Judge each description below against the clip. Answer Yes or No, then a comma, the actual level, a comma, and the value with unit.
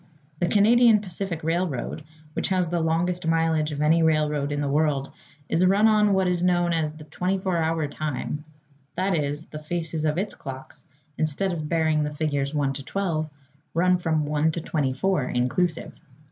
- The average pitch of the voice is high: No, medium, 160 Hz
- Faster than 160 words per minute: Yes, average, 175 wpm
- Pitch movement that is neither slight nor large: Yes, average, 3.1 semitones